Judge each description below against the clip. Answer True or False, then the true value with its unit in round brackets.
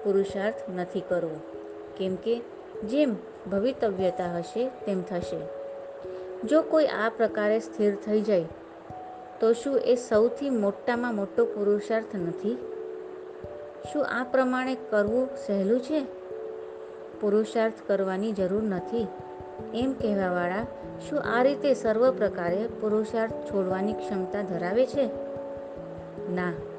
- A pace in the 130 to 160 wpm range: False (110 wpm)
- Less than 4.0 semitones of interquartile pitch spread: False (4.6 semitones)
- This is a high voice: True (215 Hz)